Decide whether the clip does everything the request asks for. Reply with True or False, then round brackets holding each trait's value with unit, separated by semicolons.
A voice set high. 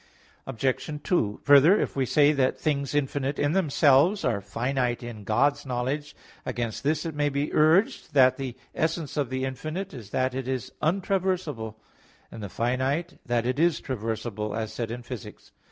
False (135 Hz)